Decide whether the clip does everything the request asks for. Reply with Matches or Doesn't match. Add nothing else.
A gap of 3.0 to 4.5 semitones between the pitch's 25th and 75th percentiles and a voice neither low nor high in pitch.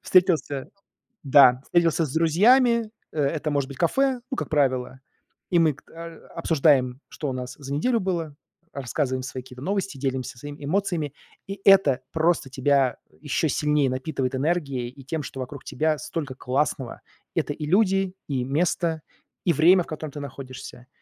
Matches